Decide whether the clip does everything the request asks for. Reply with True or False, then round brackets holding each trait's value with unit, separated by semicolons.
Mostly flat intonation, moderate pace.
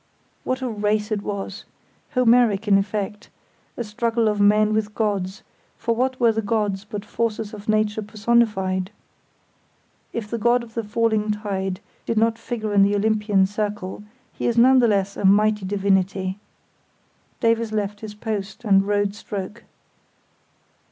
True (2.1 semitones; 150 wpm)